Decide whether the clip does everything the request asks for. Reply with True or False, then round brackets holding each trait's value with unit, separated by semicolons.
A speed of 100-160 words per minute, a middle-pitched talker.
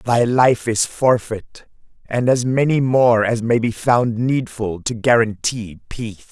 False (150 wpm; 115 Hz)